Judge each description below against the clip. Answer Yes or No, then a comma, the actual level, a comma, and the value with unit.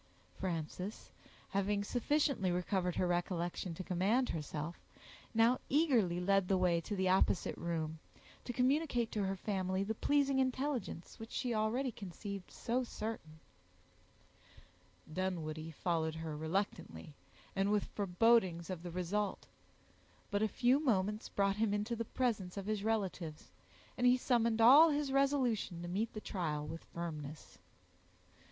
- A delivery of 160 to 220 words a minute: No, average, 140 wpm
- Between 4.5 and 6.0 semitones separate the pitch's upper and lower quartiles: Yes, average, 5.0 semitones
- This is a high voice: Yes, high, 200 Hz